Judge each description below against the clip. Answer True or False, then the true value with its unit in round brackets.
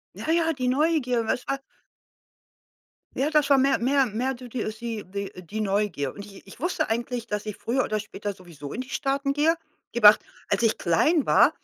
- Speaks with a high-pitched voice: True (235 Hz)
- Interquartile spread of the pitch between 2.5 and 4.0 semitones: False (4.8 semitones)